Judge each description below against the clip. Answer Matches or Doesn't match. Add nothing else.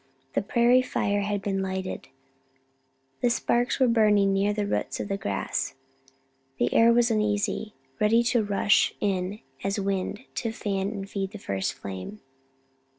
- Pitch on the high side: Matches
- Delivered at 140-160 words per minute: Matches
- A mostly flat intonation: Matches